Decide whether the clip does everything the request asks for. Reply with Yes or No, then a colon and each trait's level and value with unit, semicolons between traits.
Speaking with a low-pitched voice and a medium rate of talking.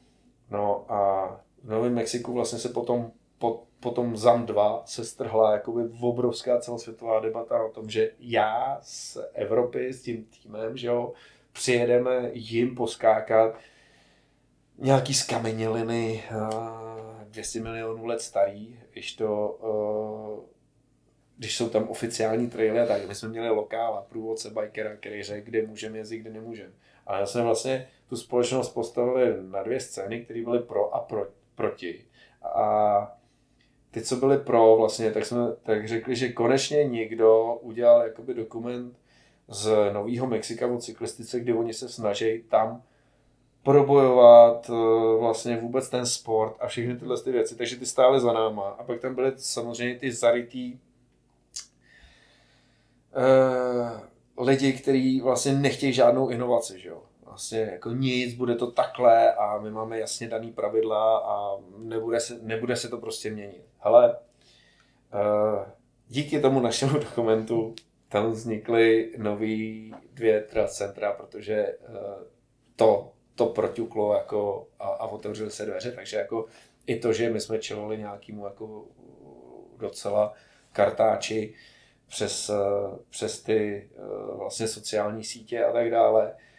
Yes: low, 115 Hz; average, 130 wpm